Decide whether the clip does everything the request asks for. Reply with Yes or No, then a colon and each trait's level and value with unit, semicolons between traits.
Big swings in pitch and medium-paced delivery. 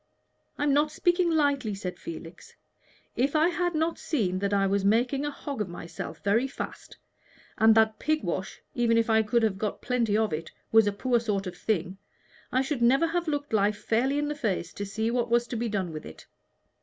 No: wide, 5.8 semitones; fast, 210 wpm